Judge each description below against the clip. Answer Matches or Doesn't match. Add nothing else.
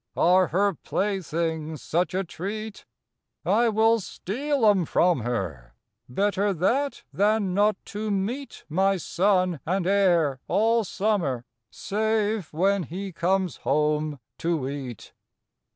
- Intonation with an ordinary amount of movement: Matches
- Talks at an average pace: Doesn't match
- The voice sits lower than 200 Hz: Matches